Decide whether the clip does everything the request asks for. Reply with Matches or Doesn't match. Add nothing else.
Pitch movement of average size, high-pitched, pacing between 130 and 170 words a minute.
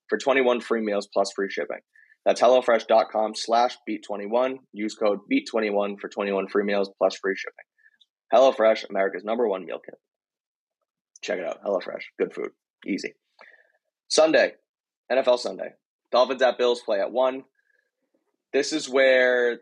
Doesn't match